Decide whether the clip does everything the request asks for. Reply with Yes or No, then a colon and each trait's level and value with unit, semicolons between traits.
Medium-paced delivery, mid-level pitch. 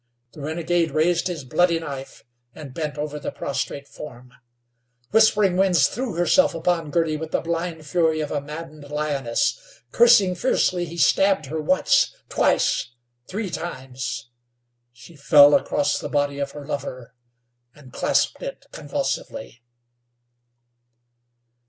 No: slow, 130 wpm; medium, 155 Hz